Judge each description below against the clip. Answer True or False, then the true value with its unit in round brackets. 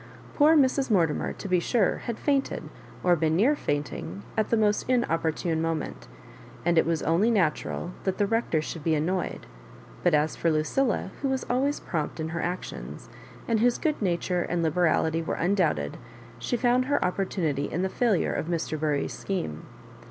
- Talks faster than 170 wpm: True (180 wpm)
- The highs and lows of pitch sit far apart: True (6.1 semitones)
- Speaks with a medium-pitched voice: True (175 Hz)